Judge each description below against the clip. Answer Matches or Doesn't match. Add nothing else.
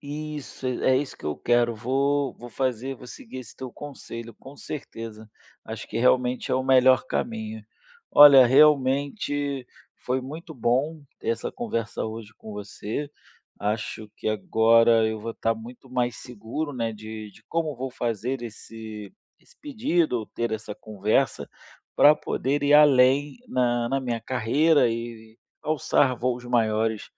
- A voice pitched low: Matches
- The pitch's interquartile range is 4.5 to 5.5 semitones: Doesn't match